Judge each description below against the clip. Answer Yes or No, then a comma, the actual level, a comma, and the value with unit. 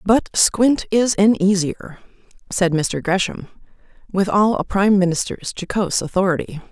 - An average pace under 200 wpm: Yes, slow, 135 wpm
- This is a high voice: Yes, high, 195 Hz